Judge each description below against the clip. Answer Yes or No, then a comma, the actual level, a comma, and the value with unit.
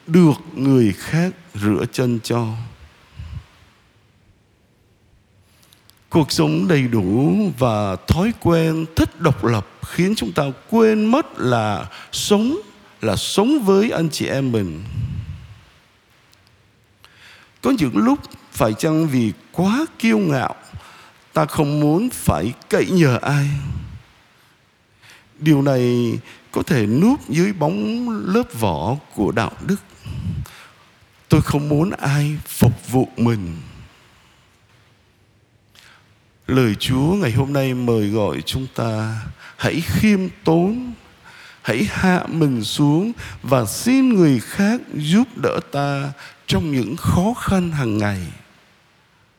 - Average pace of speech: No, slow, 115 wpm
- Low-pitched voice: Yes, low, 130 Hz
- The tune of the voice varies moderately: No, wide, 7.6 semitones